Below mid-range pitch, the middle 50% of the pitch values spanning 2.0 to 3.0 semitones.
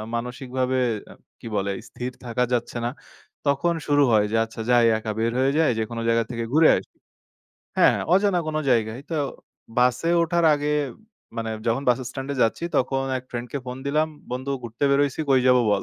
No: low, 125 Hz; average, 3.4 semitones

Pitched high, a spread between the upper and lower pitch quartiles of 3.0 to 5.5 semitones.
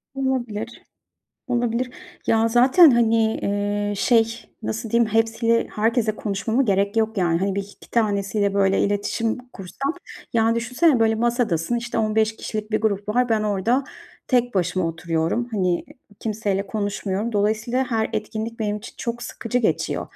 No: high, 220 Hz; narrow, 2.5 semitones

